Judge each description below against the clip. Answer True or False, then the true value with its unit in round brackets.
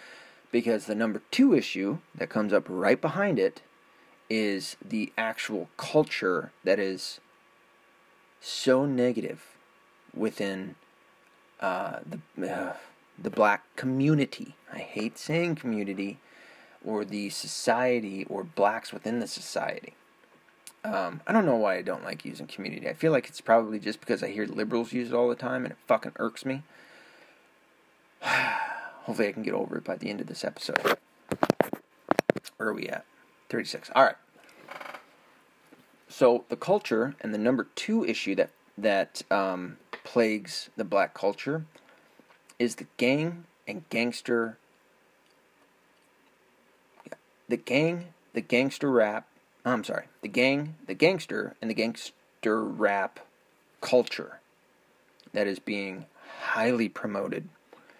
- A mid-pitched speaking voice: False (120 Hz)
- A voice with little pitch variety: False (4.9 semitones)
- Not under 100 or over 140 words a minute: True (135 wpm)